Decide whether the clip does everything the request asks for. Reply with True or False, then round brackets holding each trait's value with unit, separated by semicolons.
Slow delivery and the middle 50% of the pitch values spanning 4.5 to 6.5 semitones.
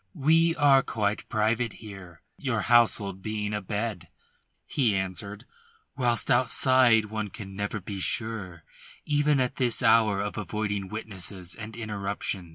False (130 wpm; 3.1 semitones)